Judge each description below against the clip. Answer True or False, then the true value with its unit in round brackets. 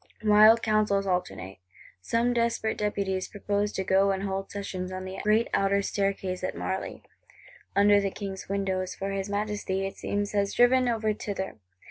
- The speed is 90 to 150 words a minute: False (160 wpm)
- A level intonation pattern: True (1.7 semitones)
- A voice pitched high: True (200 Hz)